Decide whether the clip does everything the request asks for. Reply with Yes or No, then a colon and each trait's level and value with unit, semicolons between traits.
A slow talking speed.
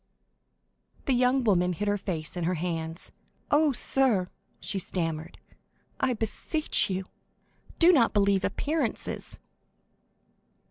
Yes: slow, 120 wpm